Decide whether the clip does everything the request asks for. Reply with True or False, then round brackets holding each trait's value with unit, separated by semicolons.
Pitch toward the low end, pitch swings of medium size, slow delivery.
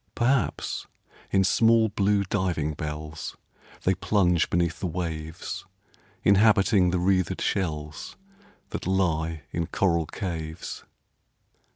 True (90 Hz; 3.6 semitones; 100 wpm)